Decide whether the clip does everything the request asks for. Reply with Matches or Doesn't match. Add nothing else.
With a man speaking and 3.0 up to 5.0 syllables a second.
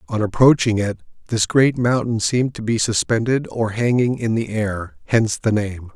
Matches